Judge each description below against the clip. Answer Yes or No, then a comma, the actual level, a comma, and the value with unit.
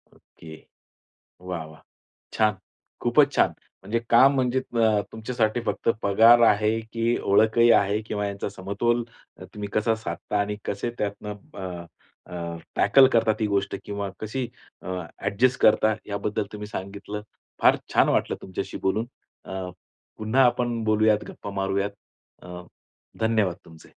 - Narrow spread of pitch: Yes, narrow, 2.3 semitones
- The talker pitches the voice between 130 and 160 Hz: No, low, 105 Hz